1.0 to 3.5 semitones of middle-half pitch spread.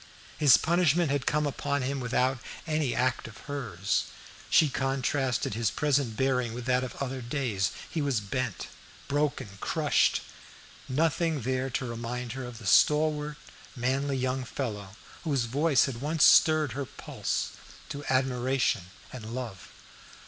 Yes: average, 2.9 semitones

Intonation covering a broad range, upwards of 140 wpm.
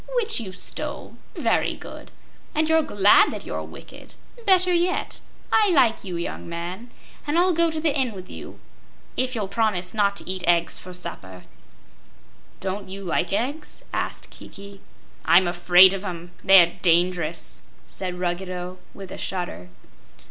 Yes: wide, 6.3 semitones; average, 155 wpm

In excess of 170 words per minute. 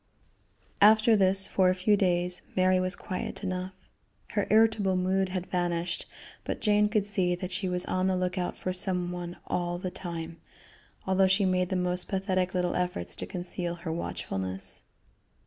No: average, 165 wpm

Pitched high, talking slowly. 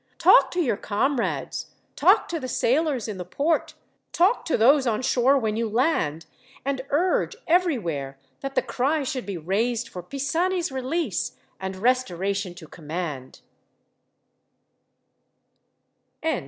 Yes: high, 245 Hz; slow, 125 wpm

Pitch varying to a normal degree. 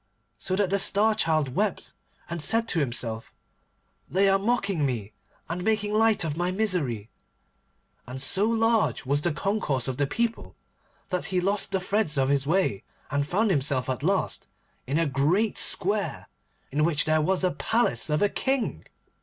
No: wide, 6.4 semitones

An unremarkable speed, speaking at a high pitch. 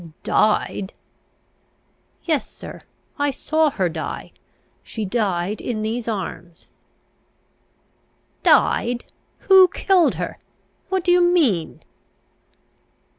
No: slow, 90 wpm; high, 240 Hz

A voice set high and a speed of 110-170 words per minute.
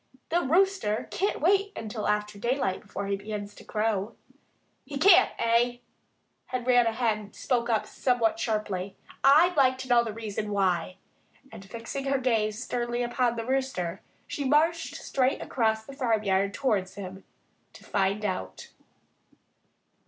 Yes: high, 230 Hz; average, 140 wpm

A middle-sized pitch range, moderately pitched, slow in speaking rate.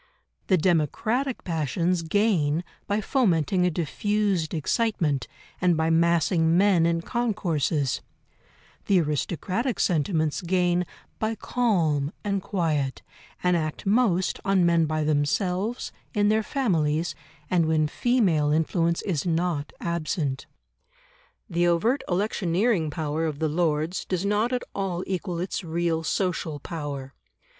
Yes: average, 4.0 semitones; medium, 170 Hz; slow, 120 wpm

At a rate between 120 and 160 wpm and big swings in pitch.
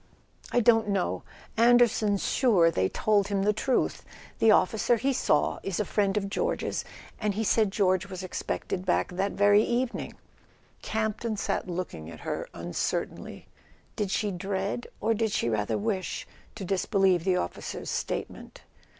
No: average, 155 wpm; average, 2.9 semitones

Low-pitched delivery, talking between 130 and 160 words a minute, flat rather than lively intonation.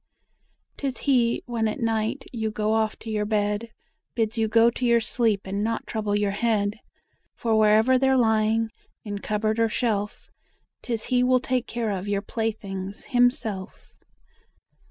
No: high, 220 Hz; average, 155 wpm; narrow, 2.0 semitones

